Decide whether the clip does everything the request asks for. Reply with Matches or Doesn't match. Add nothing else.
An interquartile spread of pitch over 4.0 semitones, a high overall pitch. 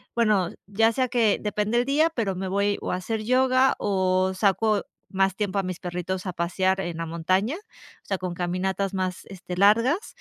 Doesn't match